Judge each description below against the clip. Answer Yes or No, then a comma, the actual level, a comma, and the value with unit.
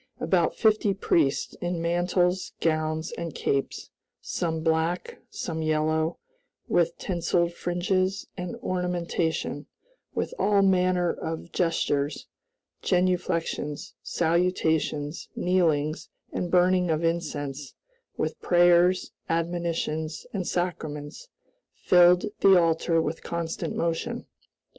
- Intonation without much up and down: Yes, narrow, 2.0 semitones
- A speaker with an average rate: No, slow, 95 wpm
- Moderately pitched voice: Yes, medium, 170 Hz